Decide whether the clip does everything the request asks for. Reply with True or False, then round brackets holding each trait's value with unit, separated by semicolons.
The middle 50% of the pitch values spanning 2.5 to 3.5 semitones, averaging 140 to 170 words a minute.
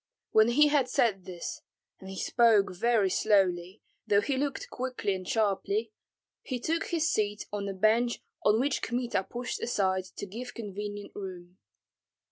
False (4.2 semitones; 155 wpm)